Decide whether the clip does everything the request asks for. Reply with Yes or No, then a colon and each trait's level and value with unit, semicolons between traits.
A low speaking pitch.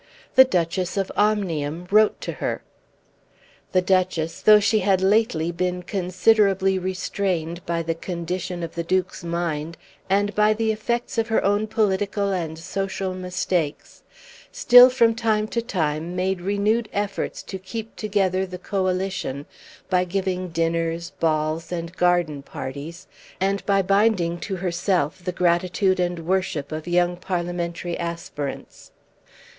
No: medium, 185 Hz